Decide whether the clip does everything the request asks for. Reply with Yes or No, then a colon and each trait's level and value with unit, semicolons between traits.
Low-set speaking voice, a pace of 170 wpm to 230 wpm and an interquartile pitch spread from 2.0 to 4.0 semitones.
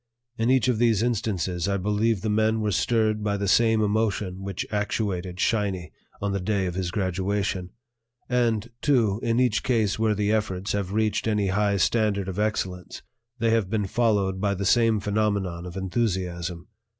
Yes: low, 105 Hz; average, 175 wpm; average, 2.7 semitones